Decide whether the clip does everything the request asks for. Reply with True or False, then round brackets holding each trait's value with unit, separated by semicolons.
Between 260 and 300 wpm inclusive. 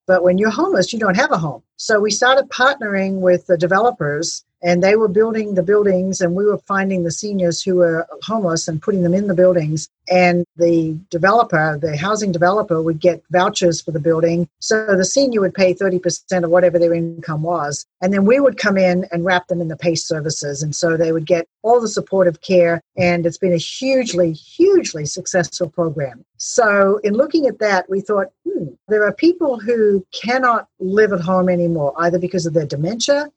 False (200 wpm)